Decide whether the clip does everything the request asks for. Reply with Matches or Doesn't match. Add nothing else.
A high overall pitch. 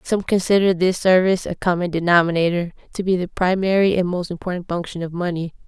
Doesn't match